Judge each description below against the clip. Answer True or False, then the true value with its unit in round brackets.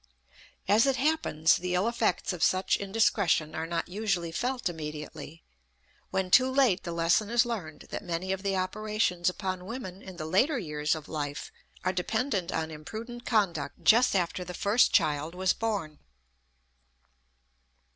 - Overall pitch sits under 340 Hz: True (185 Hz)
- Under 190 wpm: True (155 wpm)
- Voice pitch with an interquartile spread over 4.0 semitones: True (4.9 semitones)